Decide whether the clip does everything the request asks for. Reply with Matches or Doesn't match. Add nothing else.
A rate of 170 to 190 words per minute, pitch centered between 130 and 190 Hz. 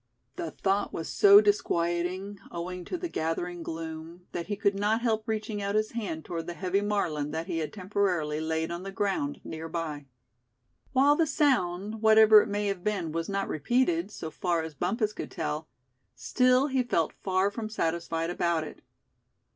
Matches